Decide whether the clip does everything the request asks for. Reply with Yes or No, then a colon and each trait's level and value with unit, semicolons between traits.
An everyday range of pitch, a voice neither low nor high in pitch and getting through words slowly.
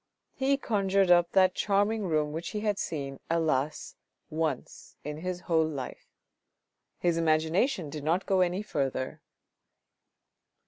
Yes: average, 4.1 semitones; medium, 170 Hz; slow, 130 wpm